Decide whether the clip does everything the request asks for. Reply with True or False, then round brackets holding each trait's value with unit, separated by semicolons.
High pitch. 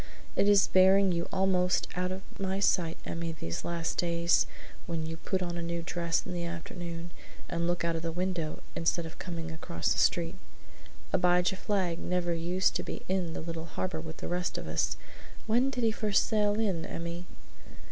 False (175 Hz)